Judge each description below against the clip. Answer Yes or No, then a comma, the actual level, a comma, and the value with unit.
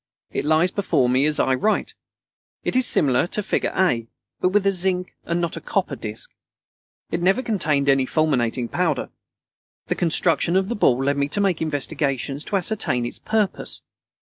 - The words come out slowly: No, average, 175 wpm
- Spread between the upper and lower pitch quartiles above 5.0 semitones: Yes, wide, 5.6 semitones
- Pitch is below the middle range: No, medium, 160 Hz